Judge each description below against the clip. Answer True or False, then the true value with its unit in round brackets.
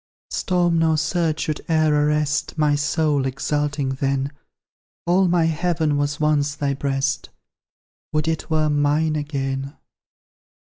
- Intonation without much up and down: True (1.8 semitones)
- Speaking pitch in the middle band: True (150 Hz)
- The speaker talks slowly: True (125 wpm)